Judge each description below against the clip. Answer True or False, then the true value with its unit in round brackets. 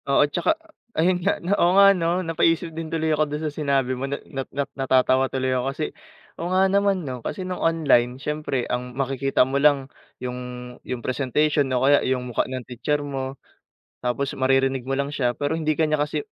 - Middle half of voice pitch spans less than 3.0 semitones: False (3.5 semitones)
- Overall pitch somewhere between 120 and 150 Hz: True (140 Hz)